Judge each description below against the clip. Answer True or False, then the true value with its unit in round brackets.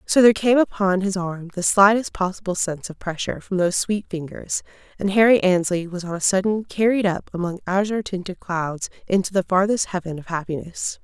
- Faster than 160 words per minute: True (190 wpm)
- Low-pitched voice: False (190 Hz)